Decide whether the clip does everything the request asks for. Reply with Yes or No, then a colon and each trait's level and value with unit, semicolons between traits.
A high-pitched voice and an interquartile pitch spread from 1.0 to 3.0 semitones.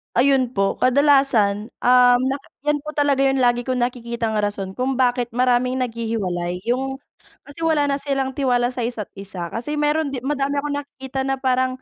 Yes: very high, 255 Hz; average, 2.7 semitones